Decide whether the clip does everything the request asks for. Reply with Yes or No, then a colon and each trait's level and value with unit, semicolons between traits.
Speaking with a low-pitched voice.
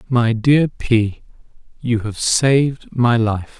Yes: low, 120 Hz